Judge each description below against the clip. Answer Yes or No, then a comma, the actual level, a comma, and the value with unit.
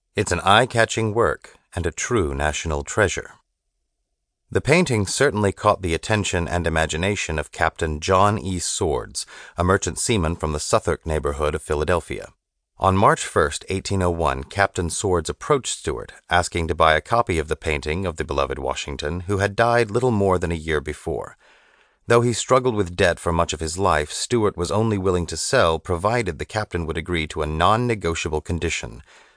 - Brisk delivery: No, average, 180 wpm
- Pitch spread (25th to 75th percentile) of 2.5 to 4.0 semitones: No, average, 4.4 semitones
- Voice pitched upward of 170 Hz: No, very low, 90 Hz